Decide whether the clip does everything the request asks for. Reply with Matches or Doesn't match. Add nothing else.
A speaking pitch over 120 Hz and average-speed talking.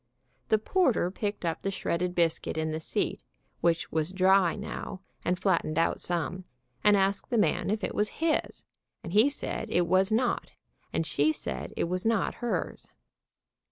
Matches